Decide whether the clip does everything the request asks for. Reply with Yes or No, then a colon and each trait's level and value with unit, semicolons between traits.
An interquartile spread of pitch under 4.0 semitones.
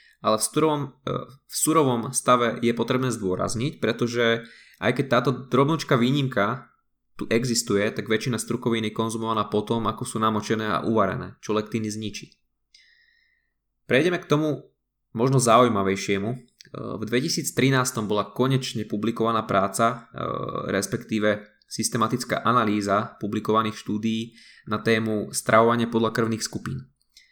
Yes: average, 2.7 semitones